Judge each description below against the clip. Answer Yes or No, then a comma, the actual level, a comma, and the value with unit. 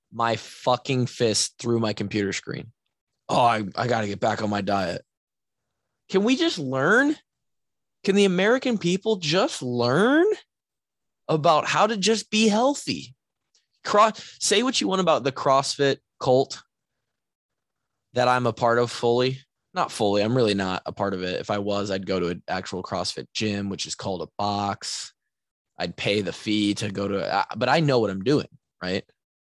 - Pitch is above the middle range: No, low, 120 Hz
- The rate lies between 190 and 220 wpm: No, average, 175 wpm